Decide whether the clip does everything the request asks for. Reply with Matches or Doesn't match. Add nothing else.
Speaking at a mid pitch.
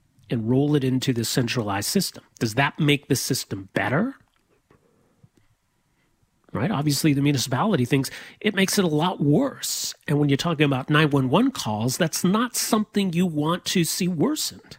Matches